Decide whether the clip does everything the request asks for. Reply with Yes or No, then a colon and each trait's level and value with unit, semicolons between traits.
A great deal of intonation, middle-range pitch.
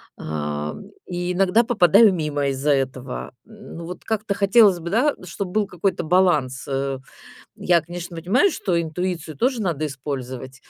Yes: wide, 6.0 semitones; medium, 175 Hz